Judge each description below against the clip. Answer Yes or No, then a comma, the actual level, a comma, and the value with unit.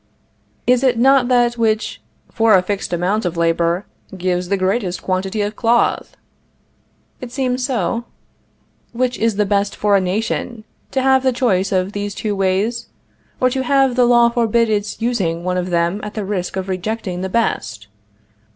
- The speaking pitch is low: No, high, 210 Hz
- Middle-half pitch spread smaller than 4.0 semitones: No, average, 4.3 semitones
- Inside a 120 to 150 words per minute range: No, average, 170 wpm